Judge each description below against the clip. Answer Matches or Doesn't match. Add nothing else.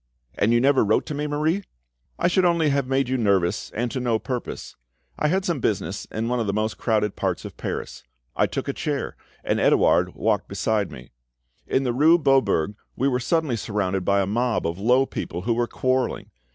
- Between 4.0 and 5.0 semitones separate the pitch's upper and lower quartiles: Matches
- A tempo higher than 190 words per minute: Matches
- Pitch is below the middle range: Matches